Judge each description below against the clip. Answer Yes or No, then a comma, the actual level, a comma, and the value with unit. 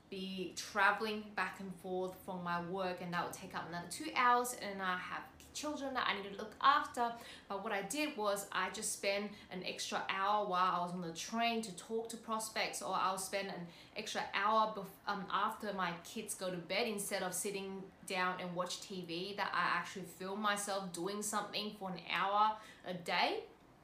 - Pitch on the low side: No, high, 195 Hz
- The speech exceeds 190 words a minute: Yes, average, 200 wpm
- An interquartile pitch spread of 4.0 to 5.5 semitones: No, average, 2.7 semitones